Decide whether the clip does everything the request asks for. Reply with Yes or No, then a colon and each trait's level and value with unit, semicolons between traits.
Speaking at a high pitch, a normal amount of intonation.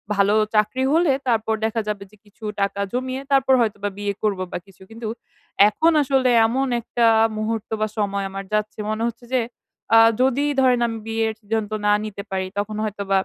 Yes: high, 220 Hz; average, 3.1 semitones